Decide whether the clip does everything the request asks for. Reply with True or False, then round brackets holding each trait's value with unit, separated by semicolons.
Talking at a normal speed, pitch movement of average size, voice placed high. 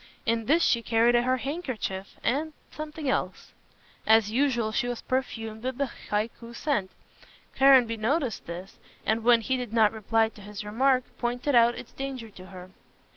True (165 wpm; 3.1 semitones; 235 Hz)